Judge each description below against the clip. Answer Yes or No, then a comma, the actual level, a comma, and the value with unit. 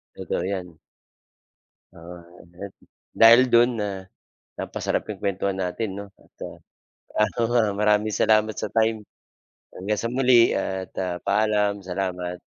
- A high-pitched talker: No, low, 100 Hz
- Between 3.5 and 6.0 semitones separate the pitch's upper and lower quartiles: No, average, 2.8 semitones